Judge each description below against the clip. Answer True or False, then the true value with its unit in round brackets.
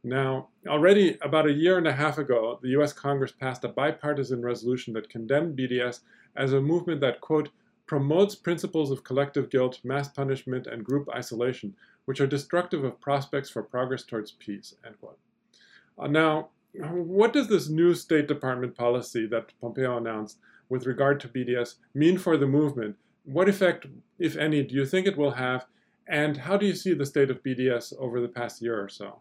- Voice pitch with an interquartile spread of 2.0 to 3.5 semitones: False (3.9 semitones)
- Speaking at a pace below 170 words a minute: False (185 wpm)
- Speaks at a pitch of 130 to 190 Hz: True (140 Hz)